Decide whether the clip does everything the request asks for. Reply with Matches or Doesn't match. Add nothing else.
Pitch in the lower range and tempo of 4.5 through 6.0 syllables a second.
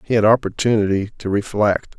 Matches